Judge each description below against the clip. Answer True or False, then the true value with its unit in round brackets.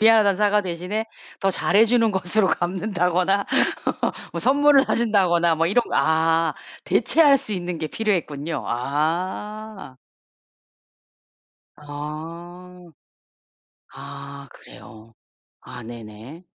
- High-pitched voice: False (180 Hz)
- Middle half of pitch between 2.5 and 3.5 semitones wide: False (5.2 semitones)